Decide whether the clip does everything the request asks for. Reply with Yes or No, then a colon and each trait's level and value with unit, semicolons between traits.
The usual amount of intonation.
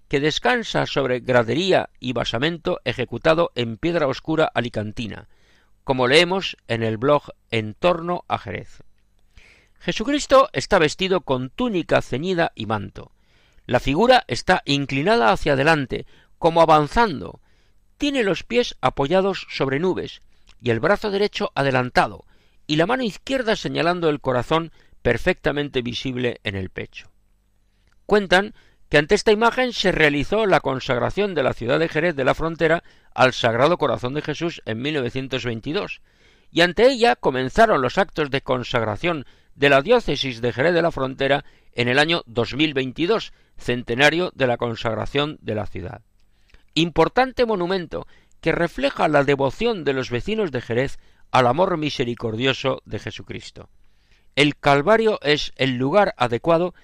No: wide, 6.8 semitones